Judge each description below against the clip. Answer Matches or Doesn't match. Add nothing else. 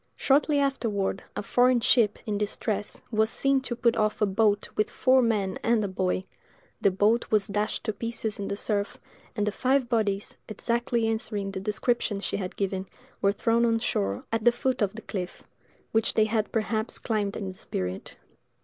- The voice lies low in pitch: Doesn't match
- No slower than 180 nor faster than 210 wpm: Matches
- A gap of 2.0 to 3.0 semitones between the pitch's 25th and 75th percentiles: Matches